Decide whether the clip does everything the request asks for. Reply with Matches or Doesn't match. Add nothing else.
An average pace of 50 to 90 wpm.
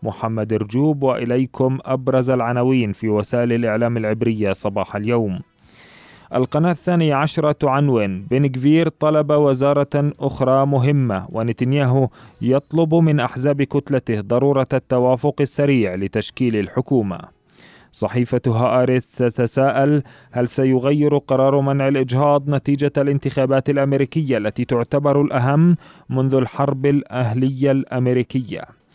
Doesn't match